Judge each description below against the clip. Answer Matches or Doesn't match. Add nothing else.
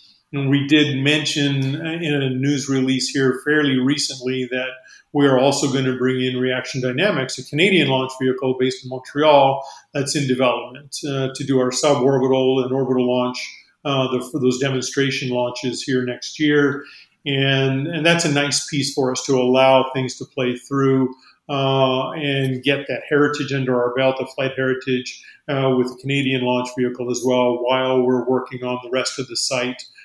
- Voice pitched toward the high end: Doesn't match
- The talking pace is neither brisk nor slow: Matches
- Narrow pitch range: Matches